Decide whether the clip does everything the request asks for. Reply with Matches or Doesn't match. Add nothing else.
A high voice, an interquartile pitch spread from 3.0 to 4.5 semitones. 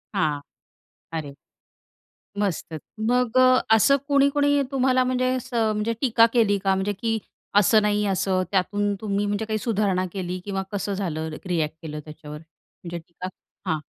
Matches